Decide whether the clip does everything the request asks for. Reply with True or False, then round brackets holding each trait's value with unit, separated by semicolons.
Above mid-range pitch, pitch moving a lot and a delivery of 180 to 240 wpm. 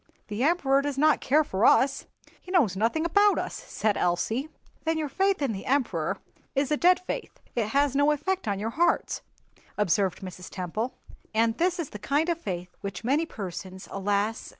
True (260 Hz; 7.6 semitones; 185 wpm)